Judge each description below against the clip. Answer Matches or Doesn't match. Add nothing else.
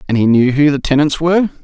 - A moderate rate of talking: Doesn't match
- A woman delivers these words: Doesn't match